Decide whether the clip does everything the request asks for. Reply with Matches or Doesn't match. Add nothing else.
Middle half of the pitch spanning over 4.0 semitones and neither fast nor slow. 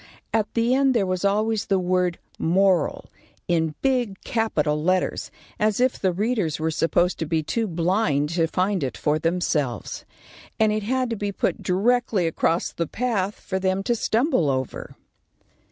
Matches